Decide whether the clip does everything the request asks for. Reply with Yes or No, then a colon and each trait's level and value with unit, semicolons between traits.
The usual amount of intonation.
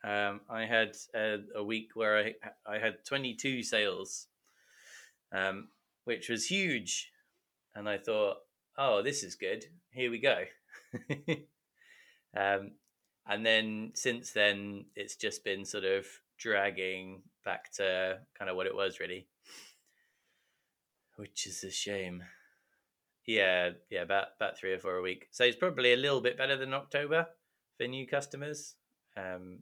No: wide, 6.7 semitones